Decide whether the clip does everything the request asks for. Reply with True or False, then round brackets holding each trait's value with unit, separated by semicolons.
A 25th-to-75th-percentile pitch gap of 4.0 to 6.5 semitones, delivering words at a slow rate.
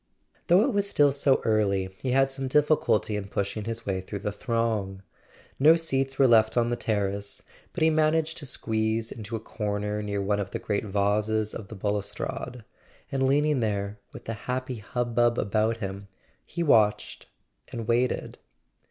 False (4.5 semitones; 170 wpm)